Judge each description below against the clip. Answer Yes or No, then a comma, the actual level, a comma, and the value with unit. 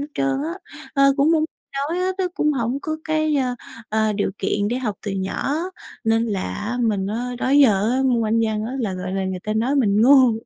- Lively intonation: No, average, 4.6 semitones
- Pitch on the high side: Yes, high, 235 Hz